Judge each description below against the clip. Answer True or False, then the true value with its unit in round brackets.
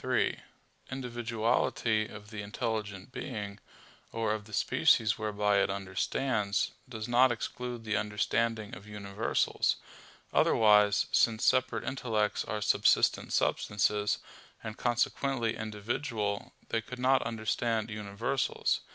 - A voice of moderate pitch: False (110 Hz)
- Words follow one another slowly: True (110 wpm)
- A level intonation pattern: True (2.2 semitones)